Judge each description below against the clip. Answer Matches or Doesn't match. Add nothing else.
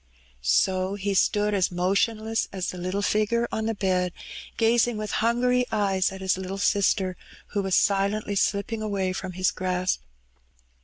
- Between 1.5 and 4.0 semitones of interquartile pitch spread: Matches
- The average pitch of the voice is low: Doesn't match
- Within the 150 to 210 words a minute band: Matches